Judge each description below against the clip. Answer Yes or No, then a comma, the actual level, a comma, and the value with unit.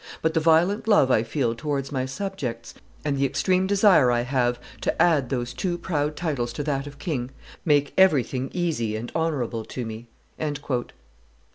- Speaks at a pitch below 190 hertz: Yes, medium, 140 Hz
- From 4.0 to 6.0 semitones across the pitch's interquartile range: Yes, average, 5.1 semitones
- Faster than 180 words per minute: No, average, 165 wpm